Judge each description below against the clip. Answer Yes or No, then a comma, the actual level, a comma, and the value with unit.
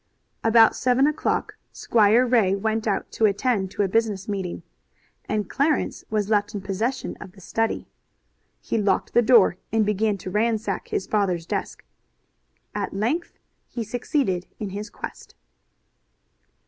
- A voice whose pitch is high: Yes, high, 215 Hz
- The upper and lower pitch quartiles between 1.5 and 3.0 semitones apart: Yes, average, 2.7 semitones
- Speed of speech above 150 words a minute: No, average, 145 wpm